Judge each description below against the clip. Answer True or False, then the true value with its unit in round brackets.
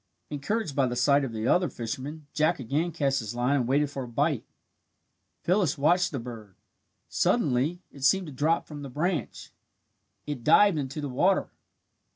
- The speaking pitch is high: False (145 Hz)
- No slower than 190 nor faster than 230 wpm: False (175 wpm)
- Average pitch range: True (4.7 semitones)